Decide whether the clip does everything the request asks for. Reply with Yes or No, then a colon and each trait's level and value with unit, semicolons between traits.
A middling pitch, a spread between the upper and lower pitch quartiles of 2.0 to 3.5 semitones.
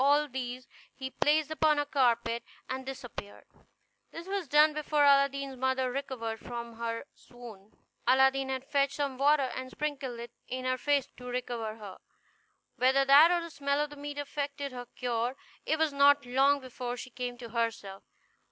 No: very high, 265 Hz; average, 2.7 semitones